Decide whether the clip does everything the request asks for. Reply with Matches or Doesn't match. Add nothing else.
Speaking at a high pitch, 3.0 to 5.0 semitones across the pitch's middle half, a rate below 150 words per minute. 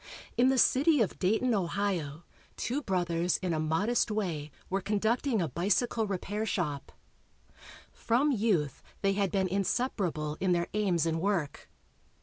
Matches